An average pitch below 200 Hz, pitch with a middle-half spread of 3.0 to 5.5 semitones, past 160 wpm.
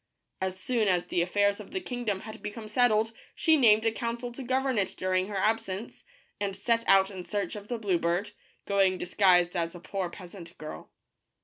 No: high, 205 Hz; average, 3.5 semitones; average, 195 wpm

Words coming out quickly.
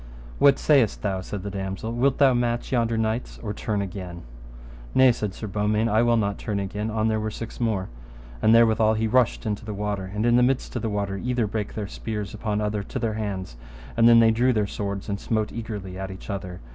Yes: fast, 220 wpm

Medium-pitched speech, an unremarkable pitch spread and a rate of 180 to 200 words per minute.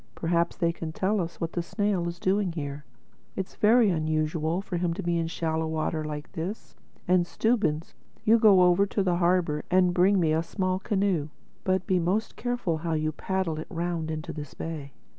Yes: medium, 170 Hz; average, 3.0 semitones; average, 190 wpm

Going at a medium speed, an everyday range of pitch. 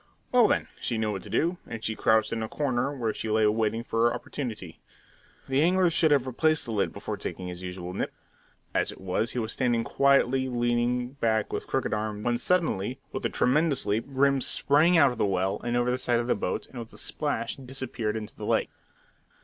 No: fast, 215 wpm; average, 3.7 semitones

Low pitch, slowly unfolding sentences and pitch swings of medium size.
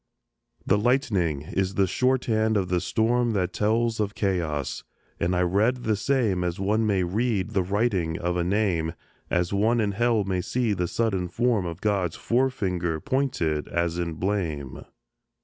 No: low, 100 Hz; average, 165 wpm; average, 4.3 semitones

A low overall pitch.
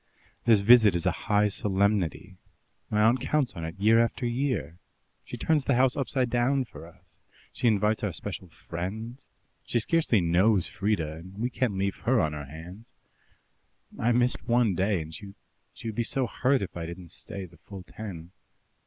Yes: low, 105 Hz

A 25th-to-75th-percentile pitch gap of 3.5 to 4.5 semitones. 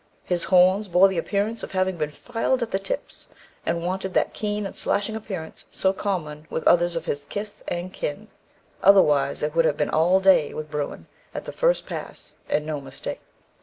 Yes: average, 4.2 semitones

